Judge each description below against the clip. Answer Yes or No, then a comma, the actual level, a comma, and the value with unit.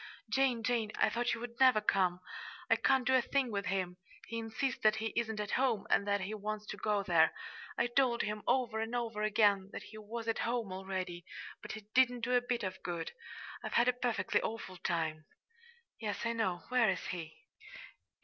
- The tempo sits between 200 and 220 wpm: Yes, fast, 205 wpm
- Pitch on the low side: No, high, 220 Hz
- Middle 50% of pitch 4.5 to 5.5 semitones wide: No, average, 3.6 semitones